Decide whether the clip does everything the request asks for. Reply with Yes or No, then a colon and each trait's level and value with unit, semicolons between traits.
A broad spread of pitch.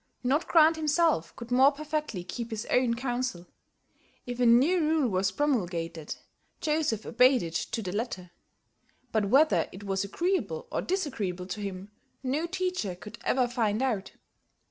Yes: wide, 7.3 semitones